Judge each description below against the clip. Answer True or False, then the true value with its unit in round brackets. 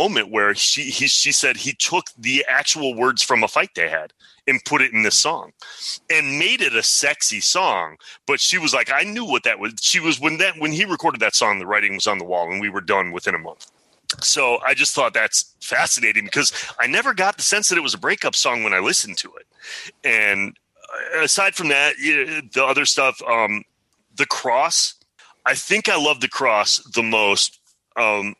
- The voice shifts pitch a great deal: True (8.1 semitones)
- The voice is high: False (145 Hz)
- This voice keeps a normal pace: False (220 wpm)